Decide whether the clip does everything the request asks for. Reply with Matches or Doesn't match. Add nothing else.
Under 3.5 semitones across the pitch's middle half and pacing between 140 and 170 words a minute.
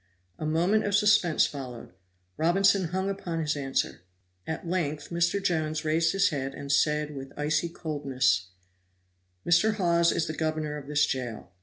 Matches